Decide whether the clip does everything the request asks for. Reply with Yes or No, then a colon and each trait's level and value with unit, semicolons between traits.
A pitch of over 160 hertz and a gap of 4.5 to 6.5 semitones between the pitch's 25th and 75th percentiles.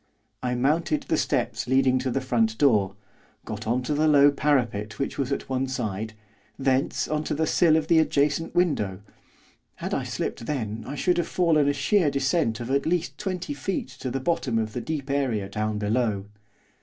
No: low, 135 Hz; average, 5.0 semitones